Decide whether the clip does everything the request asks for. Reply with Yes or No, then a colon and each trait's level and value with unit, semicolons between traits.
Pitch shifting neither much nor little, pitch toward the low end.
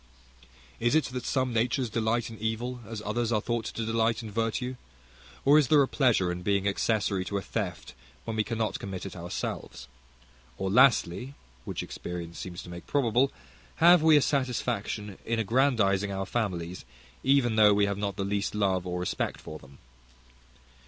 Yes: average, 3.9 semitones; low, 110 Hz